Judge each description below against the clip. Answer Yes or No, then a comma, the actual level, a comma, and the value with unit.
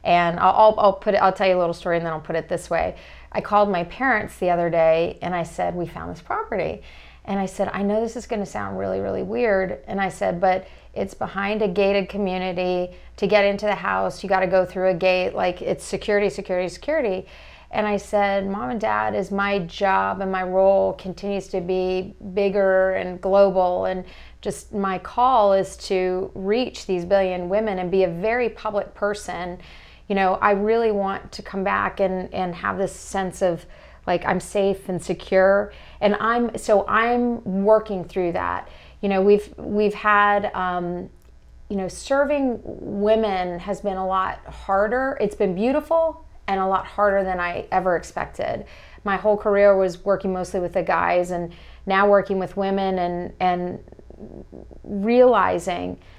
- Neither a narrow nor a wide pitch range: No, narrow, 2.1 semitones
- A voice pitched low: No, high, 195 Hz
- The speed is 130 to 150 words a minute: No, average, 190 wpm